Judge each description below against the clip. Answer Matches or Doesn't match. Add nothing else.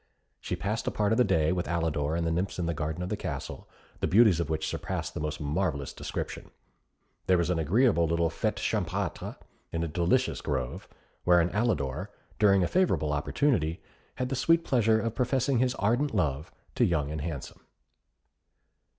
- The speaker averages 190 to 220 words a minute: Doesn't match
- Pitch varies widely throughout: Matches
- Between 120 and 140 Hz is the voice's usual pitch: Doesn't match